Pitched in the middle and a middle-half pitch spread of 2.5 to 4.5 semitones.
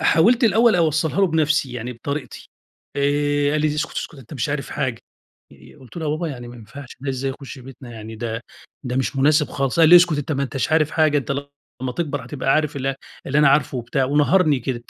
Yes: medium, 145 Hz; average, 2.9 semitones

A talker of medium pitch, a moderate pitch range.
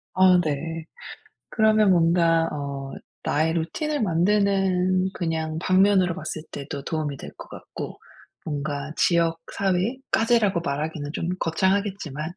Yes: medium, 170 Hz; average, 3.6 semitones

